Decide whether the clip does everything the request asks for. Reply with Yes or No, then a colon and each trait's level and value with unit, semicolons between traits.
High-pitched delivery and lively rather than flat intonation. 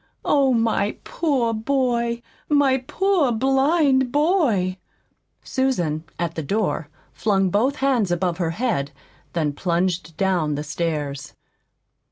Yes: high, 220 Hz; wide, 7.7 semitones